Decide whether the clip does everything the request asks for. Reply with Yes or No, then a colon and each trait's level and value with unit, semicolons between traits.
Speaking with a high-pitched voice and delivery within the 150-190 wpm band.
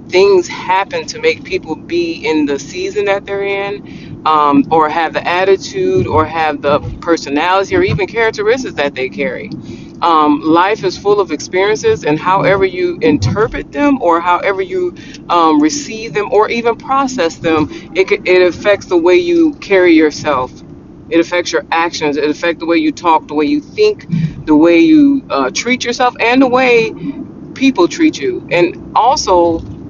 Yes: high, 195 Hz; average, 170 wpm